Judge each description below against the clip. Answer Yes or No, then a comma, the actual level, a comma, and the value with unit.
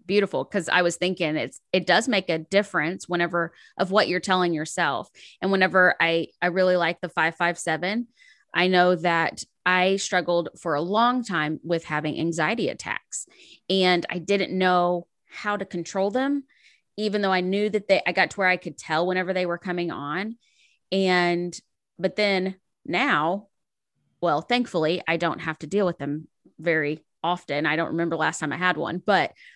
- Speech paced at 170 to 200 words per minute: Yes, average, 185 wpm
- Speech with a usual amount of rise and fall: No, narrow, 2.3 semitones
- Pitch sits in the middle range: Yes, medium, 180 Hz